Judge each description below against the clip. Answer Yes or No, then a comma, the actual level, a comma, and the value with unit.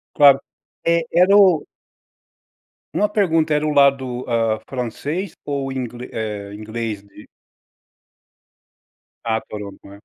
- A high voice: No, low, 130 Hz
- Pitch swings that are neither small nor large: No, wide, 5.8 semitones